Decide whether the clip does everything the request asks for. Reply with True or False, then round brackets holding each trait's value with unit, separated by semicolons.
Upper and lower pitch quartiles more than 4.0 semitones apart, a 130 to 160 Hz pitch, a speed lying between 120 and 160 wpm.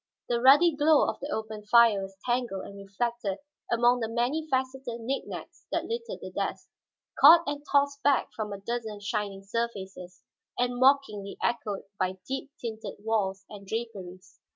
False (4.7 semitones; 235 Hz; 155 wpm)